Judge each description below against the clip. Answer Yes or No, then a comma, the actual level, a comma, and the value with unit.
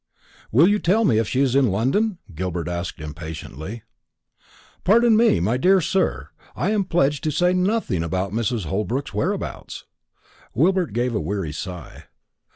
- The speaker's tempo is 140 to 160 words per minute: Yes, average, 155 wpm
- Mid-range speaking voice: No, low, 125 Hz